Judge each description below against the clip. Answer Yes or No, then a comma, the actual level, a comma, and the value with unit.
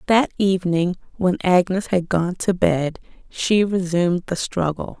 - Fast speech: No, average, 145 wpm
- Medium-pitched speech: Yes, medium, 180 Hz